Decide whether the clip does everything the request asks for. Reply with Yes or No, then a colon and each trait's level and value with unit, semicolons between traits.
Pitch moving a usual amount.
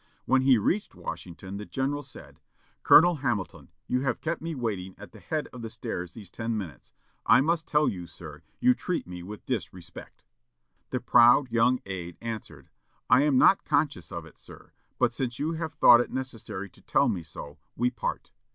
No: wide, 7.1 semitones